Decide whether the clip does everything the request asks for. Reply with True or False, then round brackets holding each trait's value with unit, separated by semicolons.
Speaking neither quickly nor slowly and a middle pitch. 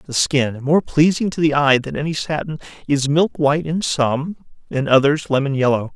True (190 wpm; 145 Hz)